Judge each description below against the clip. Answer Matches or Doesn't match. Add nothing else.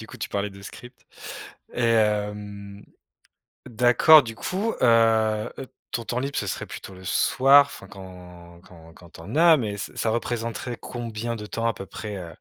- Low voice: Matches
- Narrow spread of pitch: Doesn't match